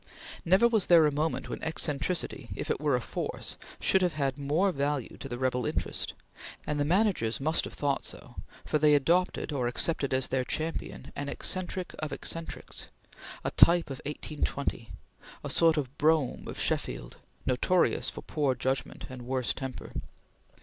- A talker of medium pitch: Yes, medium, 145 Hz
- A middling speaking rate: Yes, average, 165 wpm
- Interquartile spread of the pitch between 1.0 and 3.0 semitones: No, average, 3.9 semitones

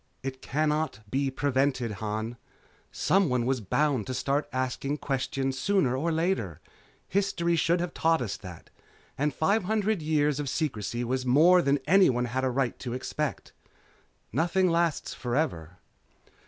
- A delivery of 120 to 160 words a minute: Yes, average, 140 wpm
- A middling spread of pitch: Yes, average, 4.6 semitones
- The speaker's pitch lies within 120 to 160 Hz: Yes, medium, 140 Hz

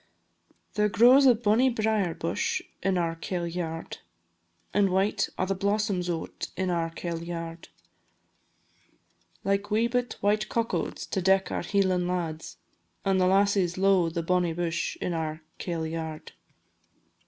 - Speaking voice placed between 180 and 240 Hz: Yes, medium, 185 Hz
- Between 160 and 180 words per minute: No, average, 140 wpm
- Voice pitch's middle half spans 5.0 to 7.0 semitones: No, average, 3.3 semitones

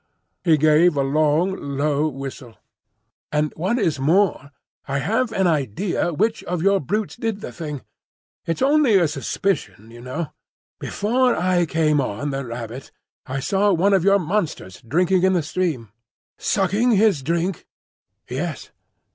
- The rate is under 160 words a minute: Yes, average, 145 wpm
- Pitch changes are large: Yes, wide, 5.9 semitones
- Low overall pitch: No, medium, 165 Hz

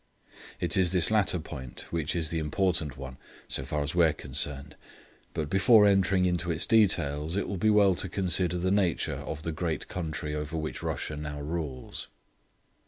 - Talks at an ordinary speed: Yes, average, 180 wpm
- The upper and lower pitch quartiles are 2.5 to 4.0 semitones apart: Yes, average, 3.7 semitones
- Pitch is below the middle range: Yes, very low, 85 Hz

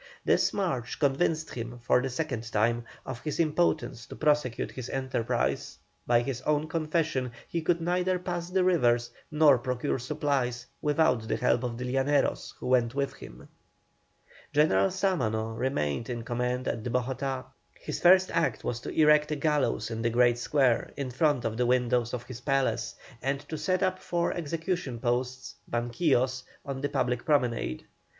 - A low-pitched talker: Yes, low, 130 Hz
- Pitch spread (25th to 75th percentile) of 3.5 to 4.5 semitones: Yes, average, 4.1 semitones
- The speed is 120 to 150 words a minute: No, average, 165 wpm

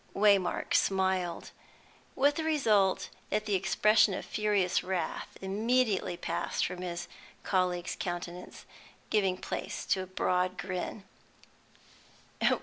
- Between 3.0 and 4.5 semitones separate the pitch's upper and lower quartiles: No, narrow, 2.6 semitones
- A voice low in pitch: No, high, 190 Hz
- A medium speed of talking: No, slow, 115 wpm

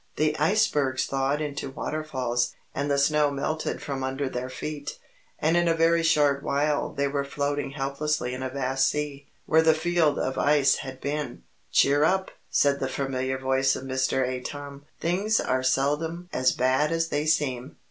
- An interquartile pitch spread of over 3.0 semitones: No, narrow, 2.5 semitones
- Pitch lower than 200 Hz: Yes, medium, 140 Hz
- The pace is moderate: Yes, average, 170 wpm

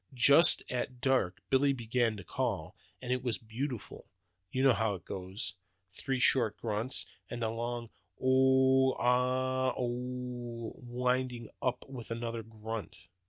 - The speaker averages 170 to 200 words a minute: No, average, 140 wpm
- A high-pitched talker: No, low, 125 Hz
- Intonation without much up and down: Yes, narrow, 2.2 semitones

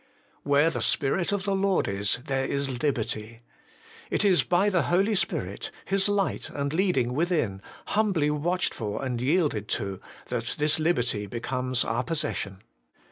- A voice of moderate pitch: Yes, medium, 145 Hz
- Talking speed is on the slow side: No, average, 155 wpm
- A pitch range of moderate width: No, wide, 7.1 semitones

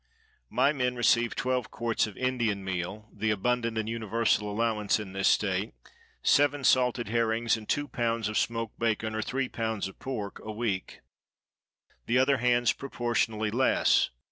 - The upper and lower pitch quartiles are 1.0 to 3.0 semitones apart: Yes, narrow, 2.4 semitones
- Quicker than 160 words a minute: No, average, 155 wpm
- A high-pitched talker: No, low, 115 Hz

